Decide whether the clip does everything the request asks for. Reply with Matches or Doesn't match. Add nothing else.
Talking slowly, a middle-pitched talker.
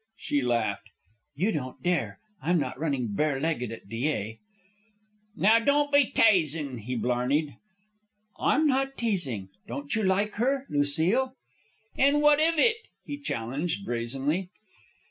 Matches